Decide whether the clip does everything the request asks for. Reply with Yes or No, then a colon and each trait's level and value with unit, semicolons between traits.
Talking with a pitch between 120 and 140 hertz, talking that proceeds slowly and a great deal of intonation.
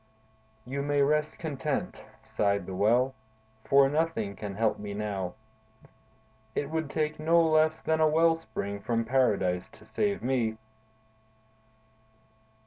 Yes: low, 135 Hz; slow, 130 wpm; wide, 6.7 semitones